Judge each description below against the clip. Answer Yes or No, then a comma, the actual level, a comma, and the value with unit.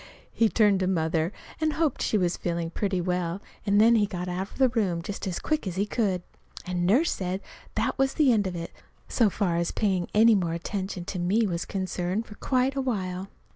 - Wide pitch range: No, average, 3.8 semitones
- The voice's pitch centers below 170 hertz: No, high, 190 Hz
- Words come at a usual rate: No, fast, 210 wpm